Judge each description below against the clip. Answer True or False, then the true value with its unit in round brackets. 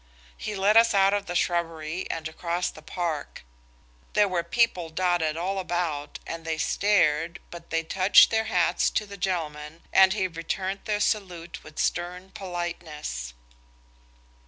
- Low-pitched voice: False (175 Hz)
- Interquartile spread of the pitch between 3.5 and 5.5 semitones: False (2.9 semitones)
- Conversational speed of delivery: True (150 wpm)